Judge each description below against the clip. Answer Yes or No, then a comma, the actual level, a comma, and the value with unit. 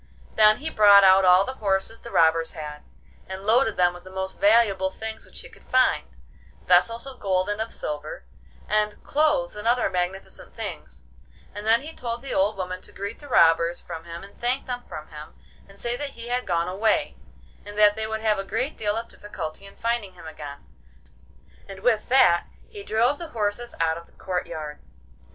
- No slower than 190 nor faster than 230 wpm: Yes, average, 195 wpm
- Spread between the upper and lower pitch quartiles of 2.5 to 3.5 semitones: No, average, 4.8 semitones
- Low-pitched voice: No, high, 205 Hz